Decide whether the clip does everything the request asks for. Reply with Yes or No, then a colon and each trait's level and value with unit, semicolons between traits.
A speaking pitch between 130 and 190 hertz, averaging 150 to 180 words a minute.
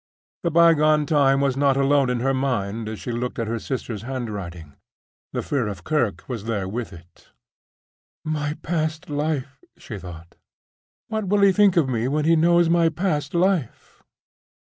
Yes: low, 135 Hz; average, 165 wpm